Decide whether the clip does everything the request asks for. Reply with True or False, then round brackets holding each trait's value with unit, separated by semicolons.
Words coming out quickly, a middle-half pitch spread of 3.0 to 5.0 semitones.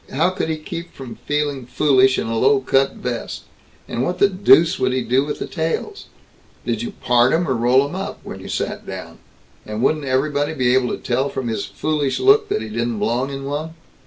True (220 wpm; 4.0 semitones)